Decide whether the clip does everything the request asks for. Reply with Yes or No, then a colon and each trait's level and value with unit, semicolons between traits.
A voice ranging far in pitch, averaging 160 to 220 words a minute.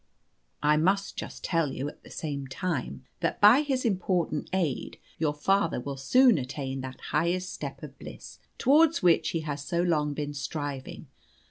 No: average, 4.6 semitones; average, 165 wpm